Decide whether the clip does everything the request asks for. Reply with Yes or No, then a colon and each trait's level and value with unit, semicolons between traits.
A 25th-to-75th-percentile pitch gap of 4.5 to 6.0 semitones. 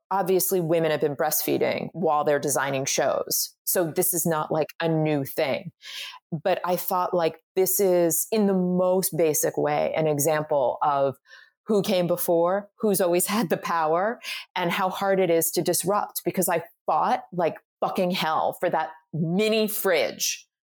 No: average, 3.0 semitones